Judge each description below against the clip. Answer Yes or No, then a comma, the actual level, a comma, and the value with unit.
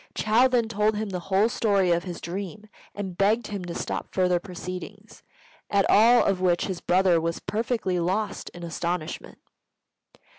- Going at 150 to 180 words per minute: Yes, average, 160 wpm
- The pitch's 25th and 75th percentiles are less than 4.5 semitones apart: Yes, average, 3.2 semitones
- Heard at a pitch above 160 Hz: Yes, high, 190 Hz